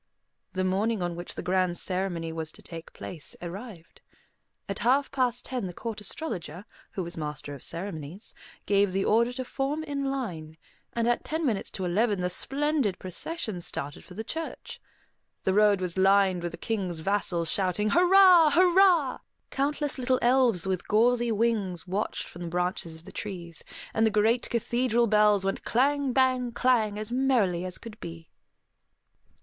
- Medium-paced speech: Yes, average, 165 wpm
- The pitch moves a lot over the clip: Yes, wide, 5.9 semitones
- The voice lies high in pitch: Yes, high, 210 Hz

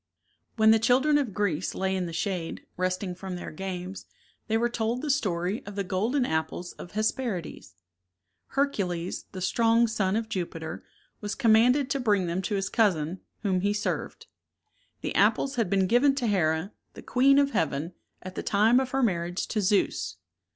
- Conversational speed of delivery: Yes, average, 180 wpm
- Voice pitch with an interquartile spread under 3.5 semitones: No, average, 4.5 semitones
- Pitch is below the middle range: No, high, 200 Hz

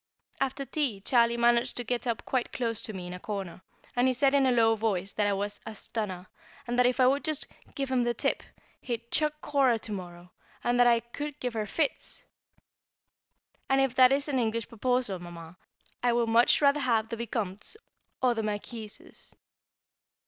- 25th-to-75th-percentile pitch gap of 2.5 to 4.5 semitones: Yes, average, 3.4 semitones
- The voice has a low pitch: No, high, 235 Hz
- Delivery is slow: No, average, 190 wpm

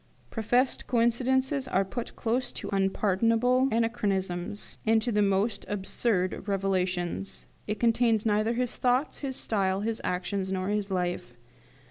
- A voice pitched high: Yes, high, 210 Hz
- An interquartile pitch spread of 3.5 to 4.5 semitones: Yes, average, 3.8 semitones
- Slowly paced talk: Yes, slow, 130 wpm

